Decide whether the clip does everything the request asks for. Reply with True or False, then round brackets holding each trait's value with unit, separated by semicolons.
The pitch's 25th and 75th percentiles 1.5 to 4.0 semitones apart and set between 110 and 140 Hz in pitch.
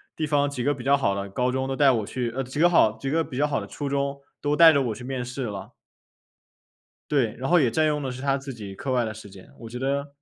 True (2.9 semitones; 135 Hz)